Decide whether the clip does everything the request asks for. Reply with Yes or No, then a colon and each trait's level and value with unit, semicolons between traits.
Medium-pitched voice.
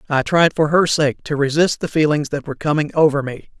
Yes: medium, 150 Hz